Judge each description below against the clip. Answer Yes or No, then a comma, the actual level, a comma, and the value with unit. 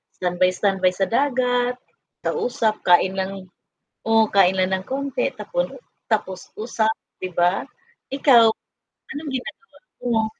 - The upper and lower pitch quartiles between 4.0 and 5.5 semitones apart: Yes, average, 4.8 semitones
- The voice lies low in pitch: No, high, 220 Hz